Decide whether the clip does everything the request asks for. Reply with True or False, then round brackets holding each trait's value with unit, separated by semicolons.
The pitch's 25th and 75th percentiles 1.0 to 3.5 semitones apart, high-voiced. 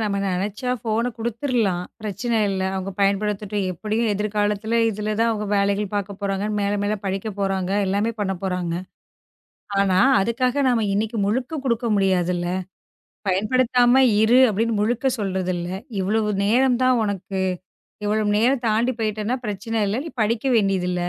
True (2.8 semitones; 210 Hz)